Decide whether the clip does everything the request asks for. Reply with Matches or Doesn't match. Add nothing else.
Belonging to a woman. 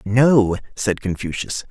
Doesn't match